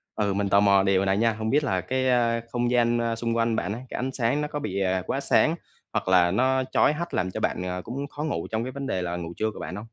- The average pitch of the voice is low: Yes, low, 115 Hz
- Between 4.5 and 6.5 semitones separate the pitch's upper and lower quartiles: Yes, average, 4.9 semitones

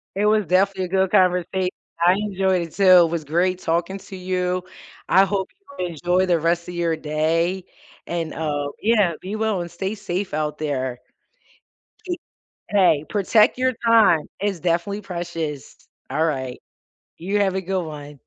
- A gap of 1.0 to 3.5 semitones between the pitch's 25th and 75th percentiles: Yes, average, 2.9 semitones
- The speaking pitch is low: No, medium, 180 Hz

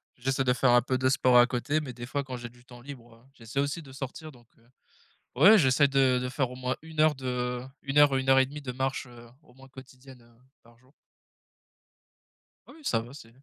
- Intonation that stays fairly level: Yes, narrow, 2.0 semitones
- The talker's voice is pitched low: Yes, low, 130 Hz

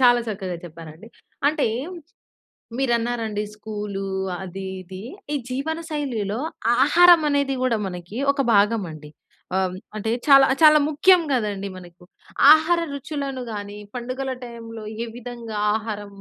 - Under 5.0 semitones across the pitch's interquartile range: No, wide, 5.4 semitones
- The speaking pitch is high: Yes, high, 230 Hz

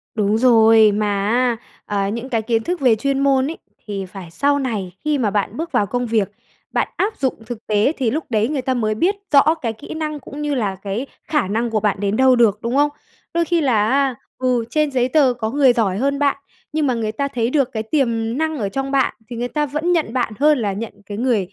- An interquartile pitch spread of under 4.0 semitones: No, average, 4.5 semitones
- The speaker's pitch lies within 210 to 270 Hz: Yes, high, 245 Hz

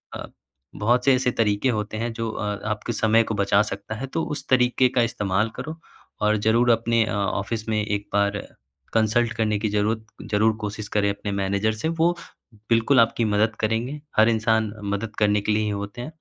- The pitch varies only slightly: Yes, narrow, 2.0 semitones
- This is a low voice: Yes, low, 110 Hz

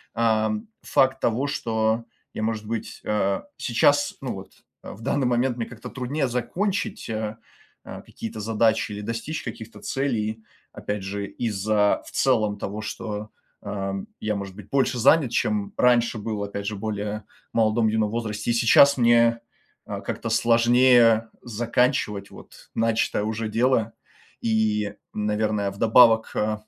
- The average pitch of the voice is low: Yes, low, 110 Hz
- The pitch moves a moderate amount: No, narrow, 2.2 semitones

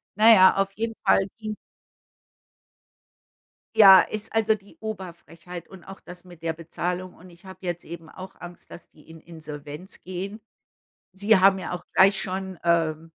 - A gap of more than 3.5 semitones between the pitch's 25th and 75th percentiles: No, narrow, 2.5 semitones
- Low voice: No, medium, 185 Hz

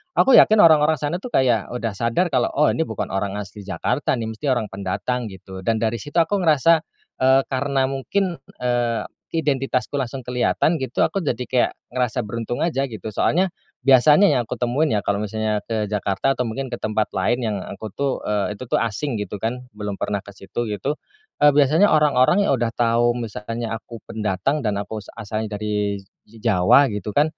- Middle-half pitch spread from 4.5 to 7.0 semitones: Yes, average, 4.8 semitones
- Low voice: Yes, low, 120 Hz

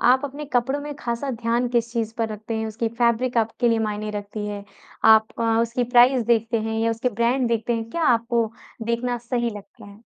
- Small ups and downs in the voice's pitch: Yes, narrow, 1.7 semitones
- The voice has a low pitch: No, high, 235 Hz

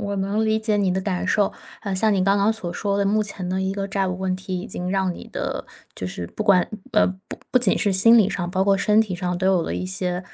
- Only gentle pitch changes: Yes, narrow, 1.8 semitones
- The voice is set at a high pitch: Yes, high, 195 Hz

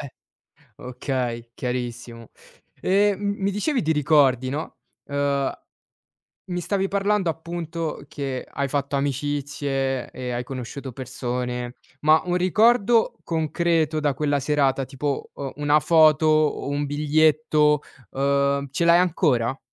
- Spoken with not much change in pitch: No, average, 3.5 semitones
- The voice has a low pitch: No, medium, 145 Hz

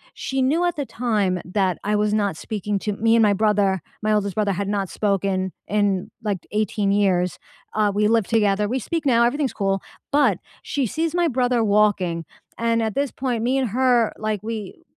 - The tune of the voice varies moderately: Yes, average, 3.3 semitones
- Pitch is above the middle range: Yes, high, 210 Hz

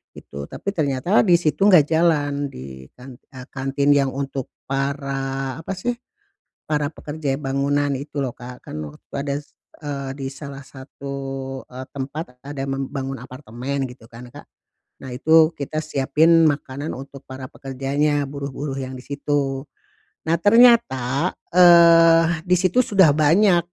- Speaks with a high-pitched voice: No, medium, 140 Hz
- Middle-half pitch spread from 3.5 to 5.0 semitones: No, average, 2.8 semitones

